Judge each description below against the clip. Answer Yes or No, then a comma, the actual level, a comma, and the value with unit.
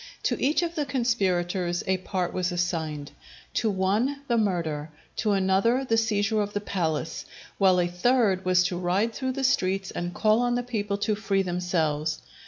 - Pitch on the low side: No, high, 195 Hz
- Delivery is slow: No, average, 180 wpm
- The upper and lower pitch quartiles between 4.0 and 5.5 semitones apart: Yes, average, 4.3 semitones